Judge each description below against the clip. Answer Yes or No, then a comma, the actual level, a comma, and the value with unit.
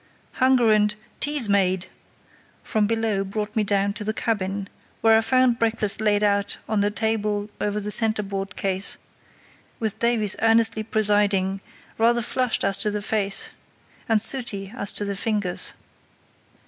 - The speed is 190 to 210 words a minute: No, average, 150 wpm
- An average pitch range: No, narrow, 1.9 semitones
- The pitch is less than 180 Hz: No, high, 210 Hz